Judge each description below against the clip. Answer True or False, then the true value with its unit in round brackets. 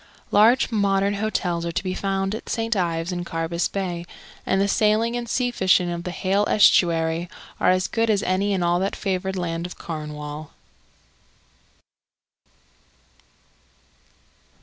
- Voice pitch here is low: False (185 Hz)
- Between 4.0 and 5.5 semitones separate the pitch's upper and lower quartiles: False (3.0 semitones)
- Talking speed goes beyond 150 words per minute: False (145 wpm)